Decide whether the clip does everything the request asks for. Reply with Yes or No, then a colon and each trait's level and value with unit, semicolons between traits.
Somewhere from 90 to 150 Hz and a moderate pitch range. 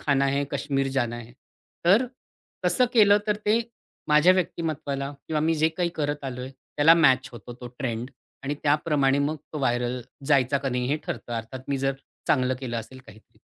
Yes: medium, 140 Hz; average, 3.3 semitones